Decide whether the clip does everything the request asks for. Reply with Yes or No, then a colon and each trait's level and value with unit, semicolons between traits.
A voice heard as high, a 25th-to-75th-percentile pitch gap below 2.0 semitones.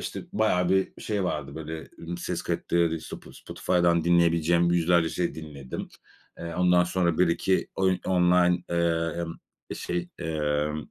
No: very low, 85 Hz; narrow, 1.5 semitones